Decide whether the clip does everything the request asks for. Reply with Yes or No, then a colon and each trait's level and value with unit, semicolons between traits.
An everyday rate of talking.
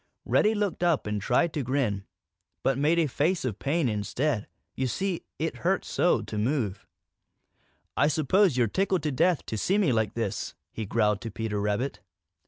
Yes: average, 180 wpm